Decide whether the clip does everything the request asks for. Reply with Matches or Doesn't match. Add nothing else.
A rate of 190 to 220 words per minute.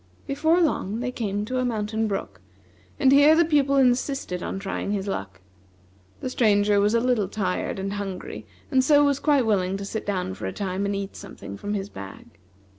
Matches